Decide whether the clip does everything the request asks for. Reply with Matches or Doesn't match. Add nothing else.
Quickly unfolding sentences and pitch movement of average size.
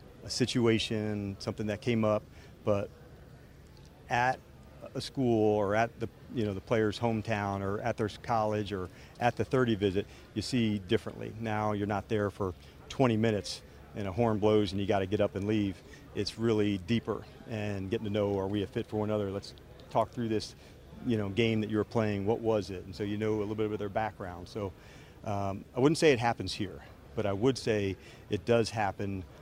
Doesn't match